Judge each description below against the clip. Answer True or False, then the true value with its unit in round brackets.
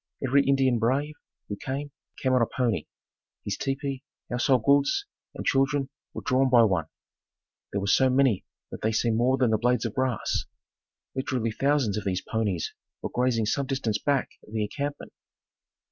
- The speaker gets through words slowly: False (170 wpm)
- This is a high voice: False (130 Hz)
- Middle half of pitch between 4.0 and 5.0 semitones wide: False (3.6 semitones)